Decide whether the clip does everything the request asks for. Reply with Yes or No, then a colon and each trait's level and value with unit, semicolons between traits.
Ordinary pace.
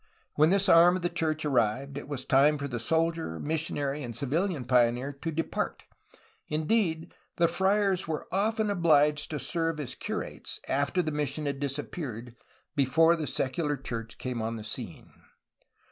Yes: average, 160 wpm